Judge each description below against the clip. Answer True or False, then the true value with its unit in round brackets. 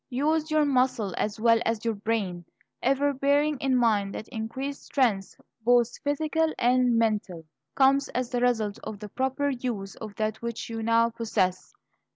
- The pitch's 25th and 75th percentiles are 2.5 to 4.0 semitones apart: True (3.7 semitones)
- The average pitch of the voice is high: True (235 Hz)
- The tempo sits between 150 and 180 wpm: True (165 wpm)